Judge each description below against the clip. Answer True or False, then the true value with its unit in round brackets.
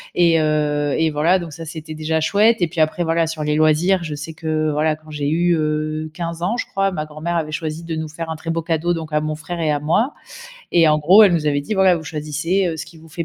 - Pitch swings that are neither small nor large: False (1.8 semitones)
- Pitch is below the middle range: False (160 Hz)